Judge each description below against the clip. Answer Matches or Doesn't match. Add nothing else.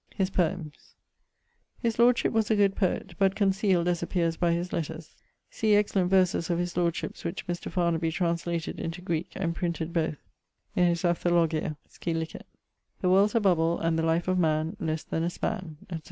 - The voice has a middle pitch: Matches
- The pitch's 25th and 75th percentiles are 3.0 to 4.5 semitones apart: Doesn't match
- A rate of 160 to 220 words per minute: Matches